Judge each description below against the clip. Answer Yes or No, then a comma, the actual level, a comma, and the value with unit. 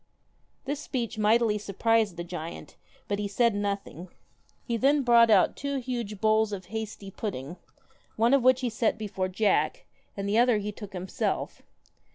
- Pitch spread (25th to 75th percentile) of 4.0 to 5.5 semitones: No, average, 3.0 semitones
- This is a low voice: No, high, 215 Hz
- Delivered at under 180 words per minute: Yes, average, 165 wpm